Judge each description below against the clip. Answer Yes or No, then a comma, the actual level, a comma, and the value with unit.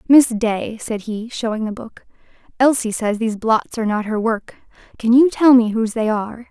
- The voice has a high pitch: Yes, high, 230 Hz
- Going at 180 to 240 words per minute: Yes, fast, 205 wpm